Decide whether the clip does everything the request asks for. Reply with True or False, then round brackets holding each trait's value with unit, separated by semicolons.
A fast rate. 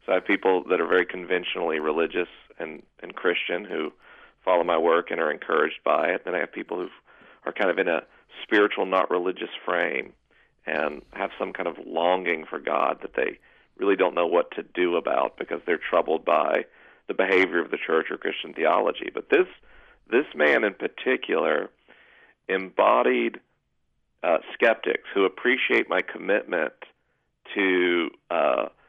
False (165 wpm)